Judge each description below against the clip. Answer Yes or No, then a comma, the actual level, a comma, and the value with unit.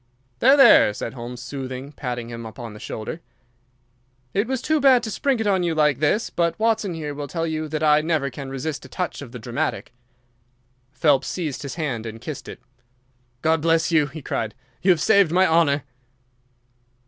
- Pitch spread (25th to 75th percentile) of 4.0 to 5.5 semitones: Yes, average, 5.2 semitones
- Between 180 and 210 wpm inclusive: Yes, average, 190 wpm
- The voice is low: No, medium, 155 Hz